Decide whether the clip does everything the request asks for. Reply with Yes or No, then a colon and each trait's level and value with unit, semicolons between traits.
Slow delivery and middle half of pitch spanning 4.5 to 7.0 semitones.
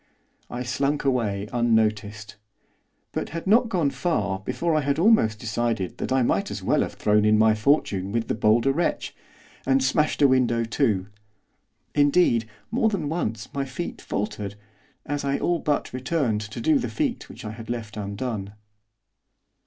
No: average, 165 wpm; average, 5.3 semitones